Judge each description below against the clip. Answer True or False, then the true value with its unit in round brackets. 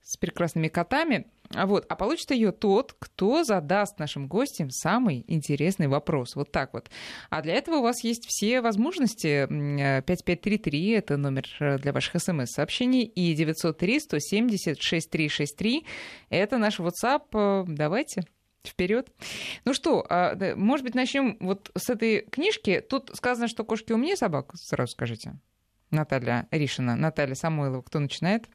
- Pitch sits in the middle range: True (180 Hz)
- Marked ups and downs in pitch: True (7.8 semitones)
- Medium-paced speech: True (135 wpm)